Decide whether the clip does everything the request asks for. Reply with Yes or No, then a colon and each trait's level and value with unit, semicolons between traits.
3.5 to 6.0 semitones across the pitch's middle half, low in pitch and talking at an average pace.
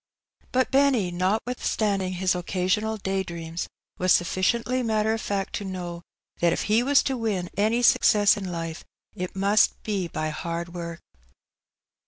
No: average, 3.9 semitones; high, 195 Hz; average, 150 wpm